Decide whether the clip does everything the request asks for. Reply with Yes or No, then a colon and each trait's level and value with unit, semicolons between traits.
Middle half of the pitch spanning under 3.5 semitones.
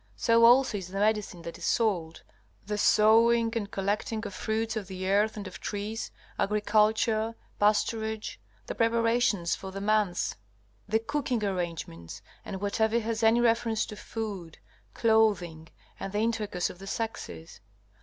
Yes: narrow, 2.6 semitones